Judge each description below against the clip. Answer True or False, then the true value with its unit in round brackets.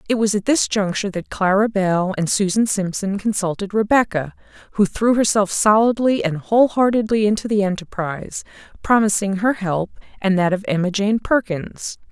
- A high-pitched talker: True (205 Hz)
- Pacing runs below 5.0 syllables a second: False (5.2 syllables/s)